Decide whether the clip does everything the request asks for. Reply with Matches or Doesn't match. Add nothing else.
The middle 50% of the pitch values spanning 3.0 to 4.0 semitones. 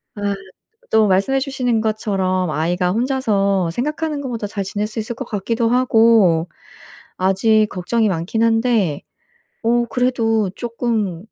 Matches